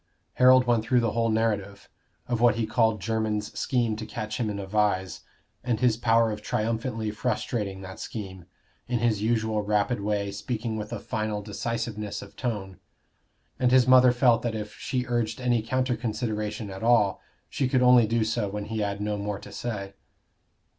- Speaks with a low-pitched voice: Yes, low, 110 Hz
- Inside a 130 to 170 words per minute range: No, average, 180 wpm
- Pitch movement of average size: No, narrow, 2.3 semitones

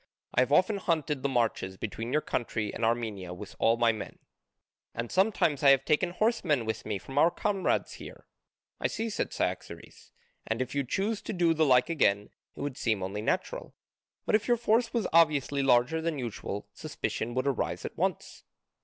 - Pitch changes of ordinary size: No, wide, 6.7 semitones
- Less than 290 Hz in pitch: Yes, low, 135 Hz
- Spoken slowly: No, average, 190 wpm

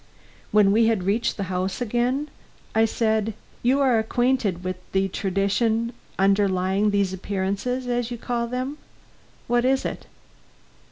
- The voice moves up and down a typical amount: Yes, average, 3.7 semitones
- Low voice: No, high, 220 Hz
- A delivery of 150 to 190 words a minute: No, slow, 135 wpm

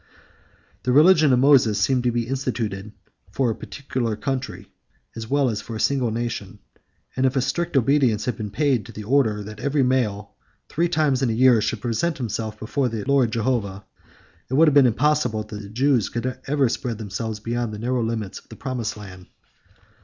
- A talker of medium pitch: No, low, 120 Hz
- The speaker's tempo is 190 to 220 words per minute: Yes, average, 200 wpm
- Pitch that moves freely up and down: No, average, 3.8 semitones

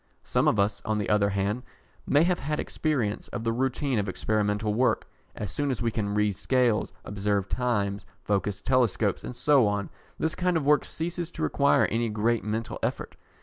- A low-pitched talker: Yes, low, 115 Hz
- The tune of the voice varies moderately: Yes, average, 4.5 semitones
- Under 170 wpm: No, average, 190 wpm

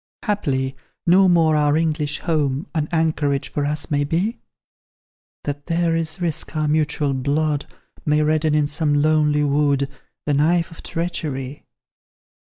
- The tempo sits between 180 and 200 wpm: No, average, 140 wpm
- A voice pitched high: No, medium, 150 Hz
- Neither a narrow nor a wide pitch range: No, narrow, 2.1 semitones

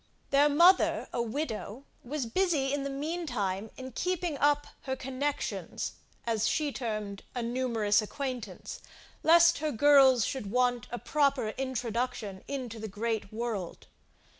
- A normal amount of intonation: Yes, average, 4.3 semitones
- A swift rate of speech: No, average, 140 wpm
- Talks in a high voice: Yes, very high, 255 Hz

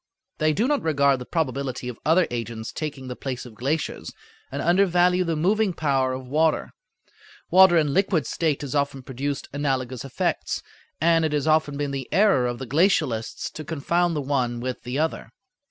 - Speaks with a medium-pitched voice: Yes, medium, 145 Hz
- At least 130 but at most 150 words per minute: No, average, 180 wpm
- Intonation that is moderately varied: Yes, average, 4.1 semitones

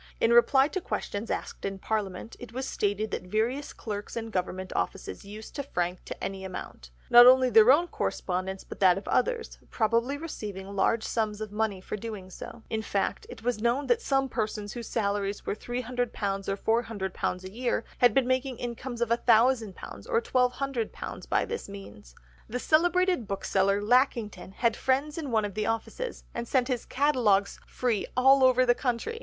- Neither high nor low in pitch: No, high, 230 Hz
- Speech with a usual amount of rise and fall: Yes, average, 4.1 semitones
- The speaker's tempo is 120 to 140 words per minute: No, average, 175 wpm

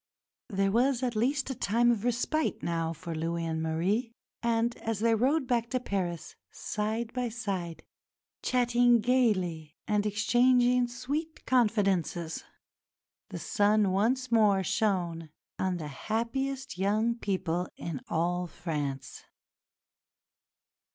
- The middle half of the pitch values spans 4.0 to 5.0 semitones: No, wide, 5.6 semitones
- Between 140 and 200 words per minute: No, slow, 120 wpm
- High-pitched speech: Yes, high, 215 Hz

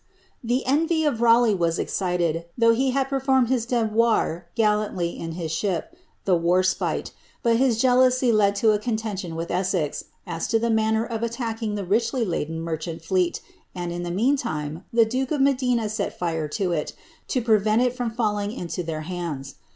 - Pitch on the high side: Yes, high, 215 Hz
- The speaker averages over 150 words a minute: Yes, average, 185 wpm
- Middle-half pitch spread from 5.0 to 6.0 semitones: Yes, wide, 5.4 semitones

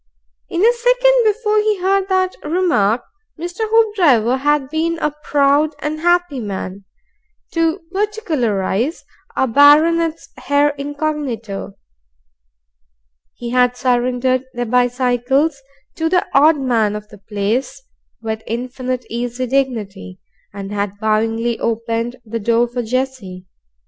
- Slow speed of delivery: Yes, slow, 120 wpm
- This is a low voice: No, very high, 260 Hz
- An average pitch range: No, wide, 6.0 semitones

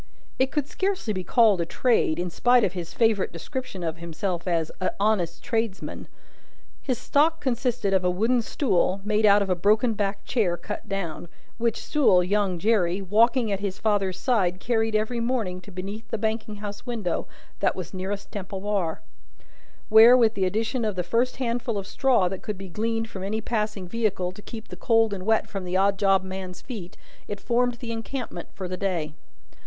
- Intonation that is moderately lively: Yes, average, 3.7 semitones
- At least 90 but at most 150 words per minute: No, average, 190 wpm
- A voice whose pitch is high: Yes, high, 205 Hz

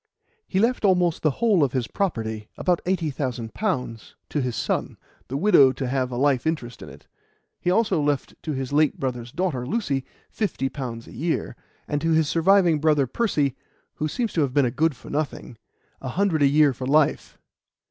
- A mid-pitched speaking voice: Yes, medium, 145 Hz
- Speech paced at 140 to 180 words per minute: No, average, 195 wpm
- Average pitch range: Yes, average, 4.8 semitones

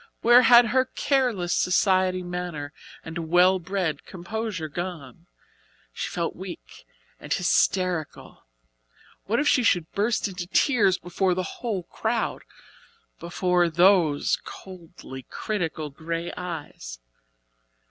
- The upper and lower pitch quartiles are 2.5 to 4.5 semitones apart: Yes, average, 3.4 semitones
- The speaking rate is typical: No, slow, 110 wpm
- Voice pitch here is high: No, medium, 180 Hz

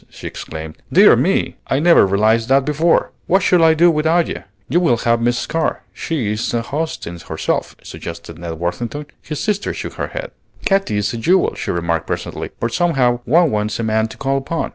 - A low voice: Yes, low, 125 Hz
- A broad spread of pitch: Yes, wide, 7.5 semitones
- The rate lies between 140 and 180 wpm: No, fast, 205 wpm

